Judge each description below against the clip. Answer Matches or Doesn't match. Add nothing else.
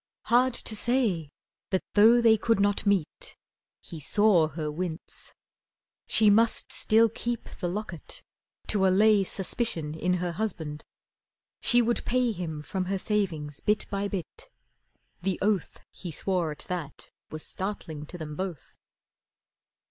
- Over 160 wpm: Doesn't match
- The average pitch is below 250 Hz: Matches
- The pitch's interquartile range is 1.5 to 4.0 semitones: Doesn't match